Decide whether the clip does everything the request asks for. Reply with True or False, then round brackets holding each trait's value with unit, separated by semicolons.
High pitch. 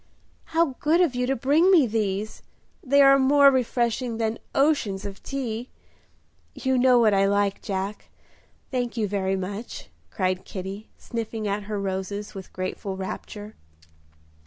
True (220 Hz)